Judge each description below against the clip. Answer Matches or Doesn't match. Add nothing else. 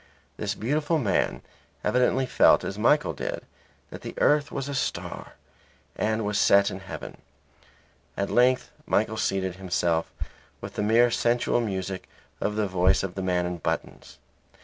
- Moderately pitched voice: Doesn't match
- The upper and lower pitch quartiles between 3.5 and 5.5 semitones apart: Matches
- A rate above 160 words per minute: Doesn't match